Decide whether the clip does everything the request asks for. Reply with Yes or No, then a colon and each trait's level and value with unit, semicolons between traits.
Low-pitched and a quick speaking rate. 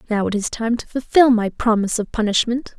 No: high, 225 Hz; fast, 215 wpm